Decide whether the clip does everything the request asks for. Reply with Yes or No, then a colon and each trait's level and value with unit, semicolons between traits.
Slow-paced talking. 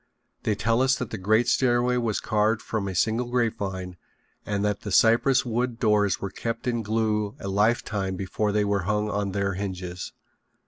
No: average, 180 wpm